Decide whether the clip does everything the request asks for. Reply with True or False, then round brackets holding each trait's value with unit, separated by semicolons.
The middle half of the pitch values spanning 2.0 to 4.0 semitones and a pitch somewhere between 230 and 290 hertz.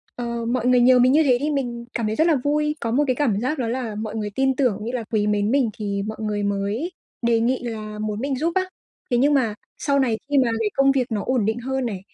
True (3.5 semitones; 240 Hz)